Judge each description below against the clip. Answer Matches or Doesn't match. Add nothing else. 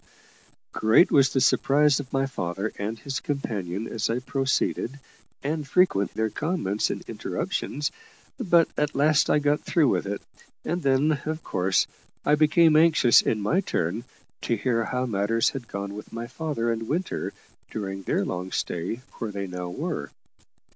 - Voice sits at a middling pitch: Doesn't match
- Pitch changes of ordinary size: Doesn't match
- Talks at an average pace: Matches